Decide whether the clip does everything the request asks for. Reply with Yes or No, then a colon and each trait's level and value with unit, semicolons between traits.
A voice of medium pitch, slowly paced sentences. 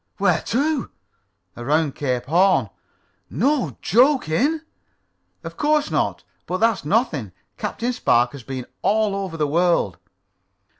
Yes: medium, 180 Hz; slow, 115 wpm